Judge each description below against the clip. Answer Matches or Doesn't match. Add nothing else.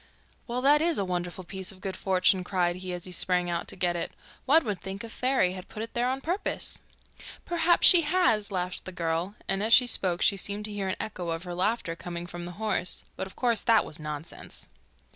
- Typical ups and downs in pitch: Matches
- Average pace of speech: Doesn't match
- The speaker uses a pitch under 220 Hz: Matches